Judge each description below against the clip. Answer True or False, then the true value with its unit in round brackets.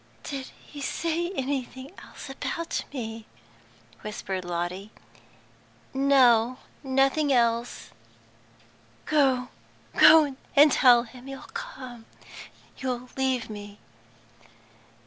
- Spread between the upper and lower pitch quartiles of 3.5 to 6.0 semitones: False (3.1 semitones)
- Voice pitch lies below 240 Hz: False (260 Hz)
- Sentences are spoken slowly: True (90 wpm)